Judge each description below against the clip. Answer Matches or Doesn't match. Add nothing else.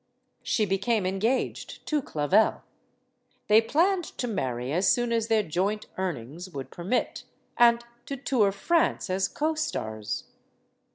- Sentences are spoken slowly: Matches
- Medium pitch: Doesn't match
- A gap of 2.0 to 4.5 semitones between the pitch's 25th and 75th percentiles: Doesn't match